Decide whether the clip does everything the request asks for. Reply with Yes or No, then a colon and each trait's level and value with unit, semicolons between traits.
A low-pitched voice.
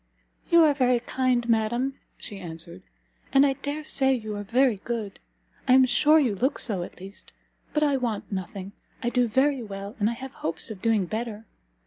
No: high, 235 Hz